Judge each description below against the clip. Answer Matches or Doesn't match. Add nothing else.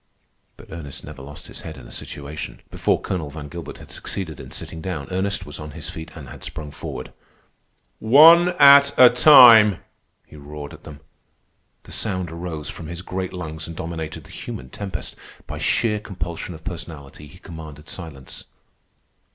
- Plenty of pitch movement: Doesn't match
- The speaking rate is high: Doesn't match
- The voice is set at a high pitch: Doesn't match